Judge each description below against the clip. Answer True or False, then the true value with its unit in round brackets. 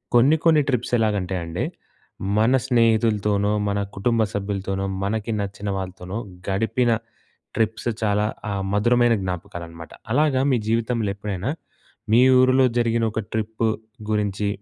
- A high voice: False (105 Hz)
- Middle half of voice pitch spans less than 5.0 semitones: True (2.9 semitones)